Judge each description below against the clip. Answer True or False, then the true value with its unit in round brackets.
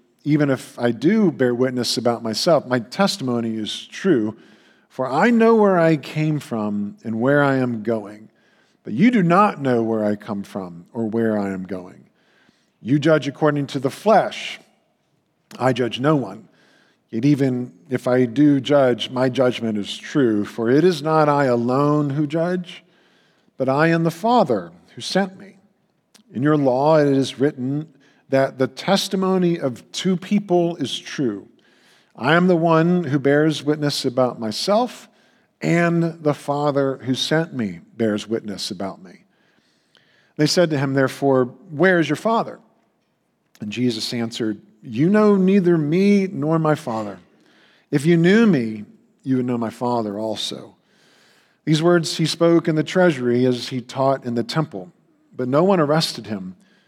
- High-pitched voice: False (140 Hz)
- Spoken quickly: False (160 wpm)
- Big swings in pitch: True (5.8 semitones)